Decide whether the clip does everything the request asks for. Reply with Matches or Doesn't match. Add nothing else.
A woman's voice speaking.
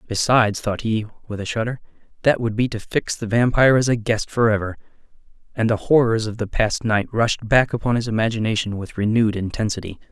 Doesn't match